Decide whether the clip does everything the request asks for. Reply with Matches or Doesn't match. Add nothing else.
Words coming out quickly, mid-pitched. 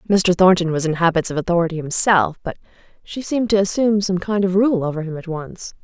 Matches